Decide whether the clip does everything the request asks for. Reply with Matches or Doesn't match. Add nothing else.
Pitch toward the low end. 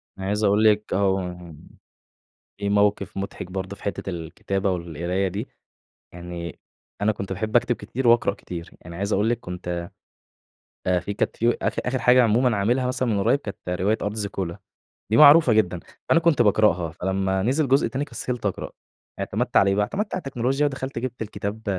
Matches